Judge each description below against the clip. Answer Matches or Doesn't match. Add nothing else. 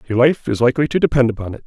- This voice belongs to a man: Matches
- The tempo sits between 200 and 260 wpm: Doesn't match